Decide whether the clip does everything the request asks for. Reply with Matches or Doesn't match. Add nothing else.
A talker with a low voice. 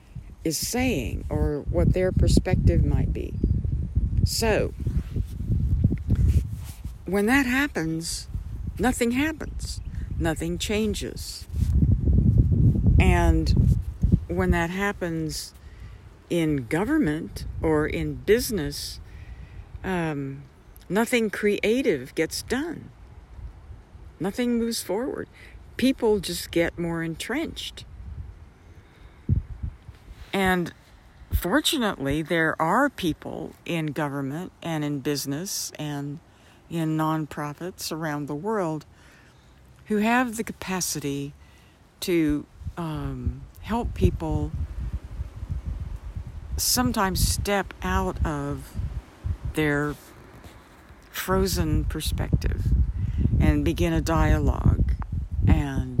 Doesn't match